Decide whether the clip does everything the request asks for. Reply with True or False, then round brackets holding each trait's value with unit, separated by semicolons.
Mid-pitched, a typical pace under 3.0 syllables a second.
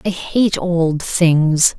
True (170 Hz; 2.4 syllables/s)